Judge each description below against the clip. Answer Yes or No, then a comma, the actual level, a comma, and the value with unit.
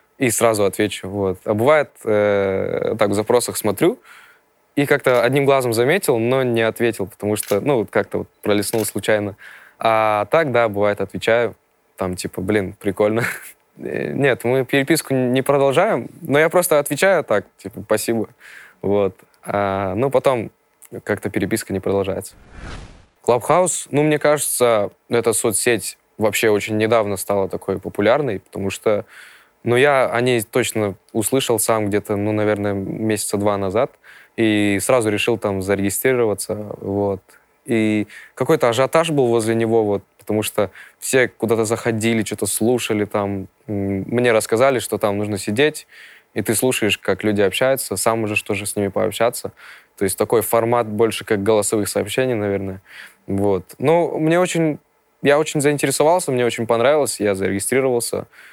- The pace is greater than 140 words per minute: Yes, average, 150 wpm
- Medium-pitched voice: No, low, 110 Hz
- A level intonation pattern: No, average, 4.0 semitones